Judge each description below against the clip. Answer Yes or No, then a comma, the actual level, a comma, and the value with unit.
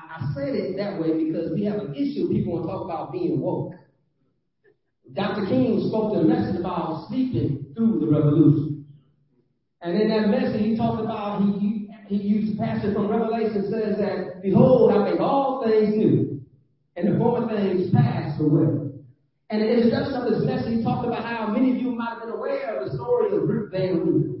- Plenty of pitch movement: Yes, wide, 6.2 semitones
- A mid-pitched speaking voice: No, high, 205 Hz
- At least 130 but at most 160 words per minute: No, average, 200 wpm